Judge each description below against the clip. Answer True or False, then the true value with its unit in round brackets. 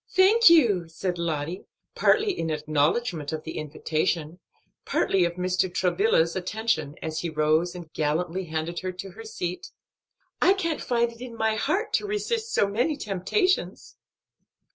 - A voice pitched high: False (180 Hz)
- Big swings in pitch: True (6.7 semitones)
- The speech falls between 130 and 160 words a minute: True (150 wpm)